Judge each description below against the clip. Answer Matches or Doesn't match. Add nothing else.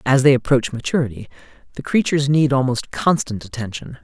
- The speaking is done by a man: Matches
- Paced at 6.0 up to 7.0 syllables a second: Doesn't match